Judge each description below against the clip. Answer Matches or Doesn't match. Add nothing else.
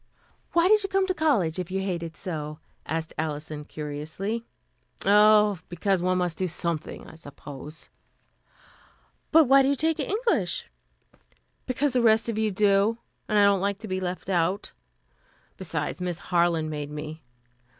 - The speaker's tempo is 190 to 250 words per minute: Doesn't match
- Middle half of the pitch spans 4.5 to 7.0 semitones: Matches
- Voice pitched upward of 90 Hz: Matches